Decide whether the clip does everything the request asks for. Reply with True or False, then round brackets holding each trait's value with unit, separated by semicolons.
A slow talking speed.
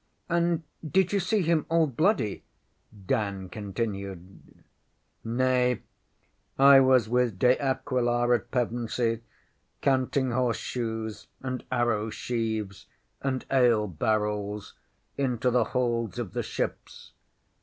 True (110 wpm)